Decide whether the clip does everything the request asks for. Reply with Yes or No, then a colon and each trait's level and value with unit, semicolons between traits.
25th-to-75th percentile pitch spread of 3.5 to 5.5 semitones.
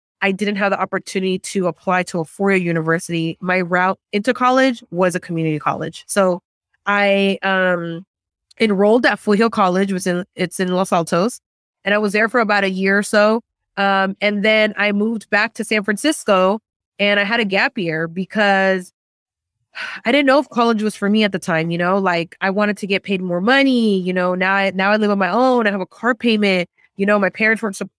No: narrow, 2.6 semitones